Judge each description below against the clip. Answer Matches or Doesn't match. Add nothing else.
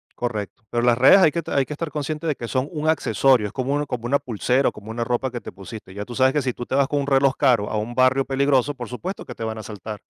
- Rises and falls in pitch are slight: Doesn't match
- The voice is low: Matches